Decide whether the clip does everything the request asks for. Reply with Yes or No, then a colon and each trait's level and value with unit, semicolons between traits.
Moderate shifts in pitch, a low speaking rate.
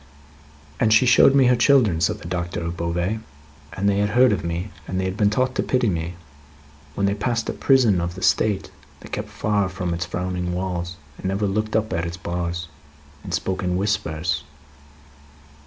No: average, 3.7 semitones; average, 190 wpm